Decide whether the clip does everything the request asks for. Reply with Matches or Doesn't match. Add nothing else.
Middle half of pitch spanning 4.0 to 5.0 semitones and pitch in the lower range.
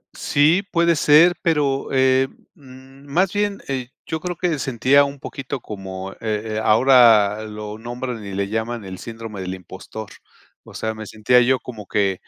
Matches